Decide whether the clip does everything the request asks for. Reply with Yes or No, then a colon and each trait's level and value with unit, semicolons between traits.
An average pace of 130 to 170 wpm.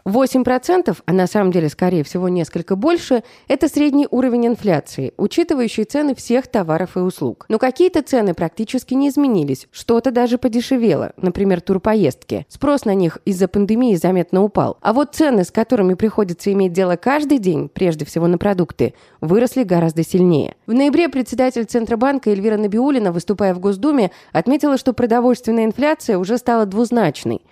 Yes: average, 155 wpm